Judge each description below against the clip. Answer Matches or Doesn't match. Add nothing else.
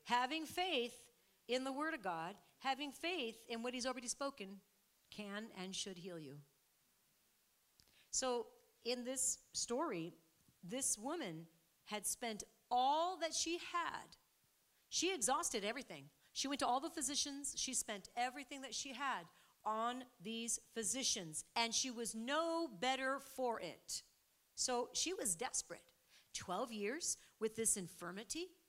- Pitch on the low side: Doesn't match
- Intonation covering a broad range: Doesn't match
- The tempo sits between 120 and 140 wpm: Matches